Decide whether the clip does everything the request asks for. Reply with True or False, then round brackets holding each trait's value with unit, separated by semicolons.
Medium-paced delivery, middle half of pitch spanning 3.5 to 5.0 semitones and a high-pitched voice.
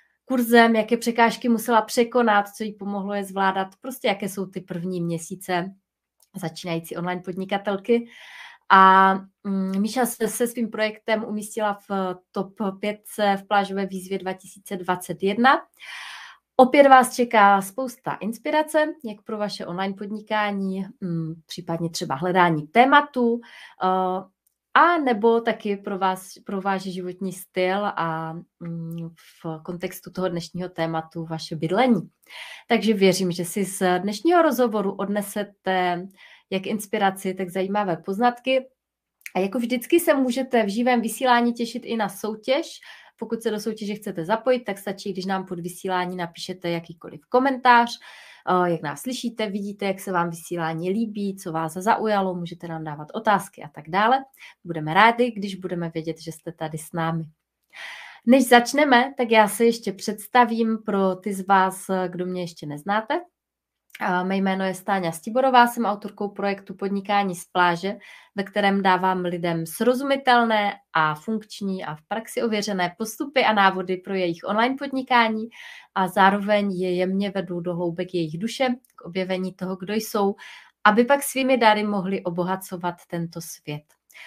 True (140 wpm; 4.0 semitones; 200 Hz)